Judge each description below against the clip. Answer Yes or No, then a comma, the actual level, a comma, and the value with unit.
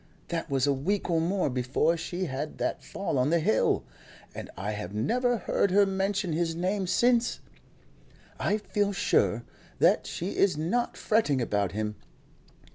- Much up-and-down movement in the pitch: Yes, wide, 7.1 semitones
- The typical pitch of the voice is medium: Yes, medium, 170 Hz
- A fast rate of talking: No, average, 160 wpm